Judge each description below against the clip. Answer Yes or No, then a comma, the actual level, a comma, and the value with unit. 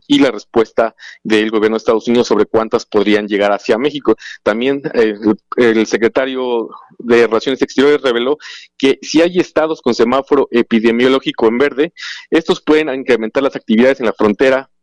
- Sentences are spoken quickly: No, average, 160 wpm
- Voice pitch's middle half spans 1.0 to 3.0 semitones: No, average, 4.3 semitones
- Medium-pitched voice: No, low, 120 Hz